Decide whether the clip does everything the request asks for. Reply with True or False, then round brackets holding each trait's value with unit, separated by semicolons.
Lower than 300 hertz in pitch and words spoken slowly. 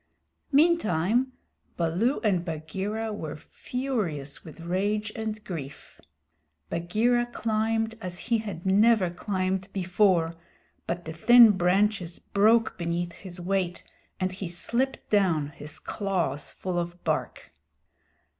True (190 Hz; 115 wpm)